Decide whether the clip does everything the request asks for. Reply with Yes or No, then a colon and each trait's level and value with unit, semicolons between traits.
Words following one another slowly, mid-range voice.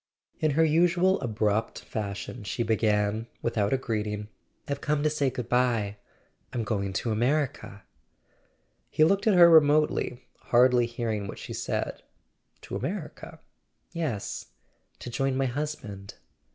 No: slow, 130 wpm; low, 120 Hz